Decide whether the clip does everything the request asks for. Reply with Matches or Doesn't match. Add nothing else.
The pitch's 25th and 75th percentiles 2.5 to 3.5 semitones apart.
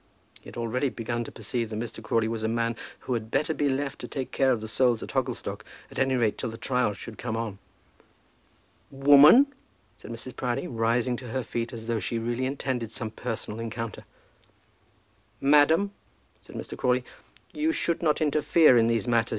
Matches